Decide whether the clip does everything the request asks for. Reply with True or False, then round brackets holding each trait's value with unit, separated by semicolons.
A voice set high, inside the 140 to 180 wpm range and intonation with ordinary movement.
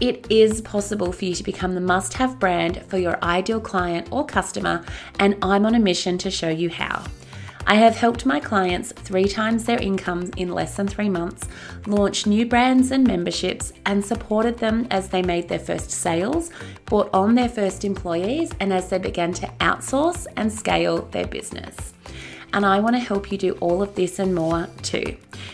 False (195 Hz; 190 wpm; 4.0 semitones)